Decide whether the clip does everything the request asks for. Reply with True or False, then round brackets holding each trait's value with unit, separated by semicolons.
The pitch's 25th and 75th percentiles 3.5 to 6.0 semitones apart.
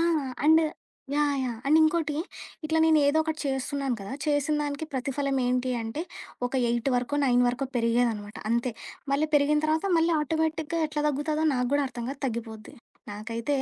True (4.0 semitones)